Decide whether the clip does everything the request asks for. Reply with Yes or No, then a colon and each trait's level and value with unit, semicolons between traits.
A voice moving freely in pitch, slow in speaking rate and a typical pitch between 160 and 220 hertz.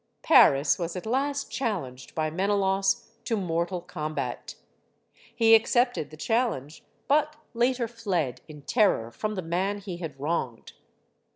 Yes: wide, 6.6 semitones; slow, 130 wpm; high, 190 Hz